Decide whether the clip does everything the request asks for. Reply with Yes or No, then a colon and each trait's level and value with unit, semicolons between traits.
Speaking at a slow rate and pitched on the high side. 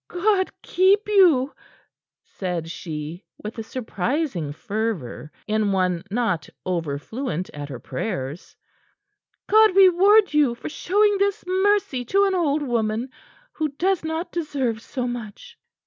Yes: slow, 130 wpm; very high, 250 Hz